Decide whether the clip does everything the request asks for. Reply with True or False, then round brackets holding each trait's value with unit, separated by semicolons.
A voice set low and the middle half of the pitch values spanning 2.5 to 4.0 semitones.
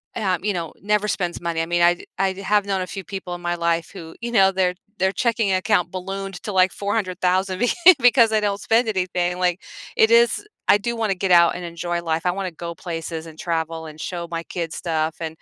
False (185 Hz; 2.8 semitones)